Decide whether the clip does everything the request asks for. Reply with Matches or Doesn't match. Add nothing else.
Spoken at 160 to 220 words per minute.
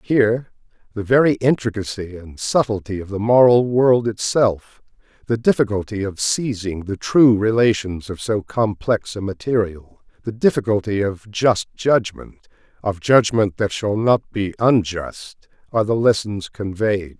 Doesn't match